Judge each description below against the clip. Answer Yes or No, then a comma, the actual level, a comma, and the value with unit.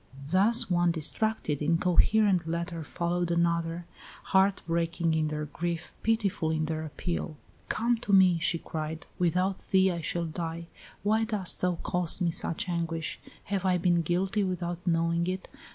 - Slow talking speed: No, average, 150 wpm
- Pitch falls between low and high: Yes, medium, 175 Hz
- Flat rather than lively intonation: Yes, narrow, 2.3 semitones